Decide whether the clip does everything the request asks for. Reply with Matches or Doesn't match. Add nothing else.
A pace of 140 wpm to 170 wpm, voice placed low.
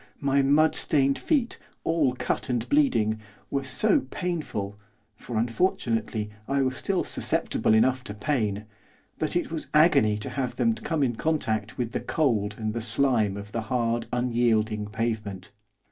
Matches